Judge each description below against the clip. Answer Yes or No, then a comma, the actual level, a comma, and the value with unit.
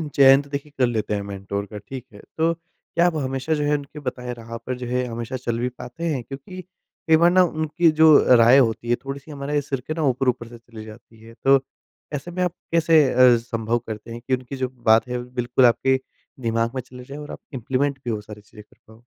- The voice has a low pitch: Yes, low, 130 Hz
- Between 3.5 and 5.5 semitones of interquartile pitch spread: Yes, average, 3.9 semitones